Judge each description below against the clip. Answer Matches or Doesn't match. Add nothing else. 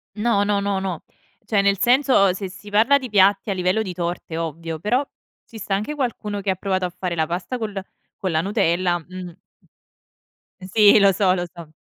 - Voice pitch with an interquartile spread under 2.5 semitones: Doesn't match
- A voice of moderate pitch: Doesn't match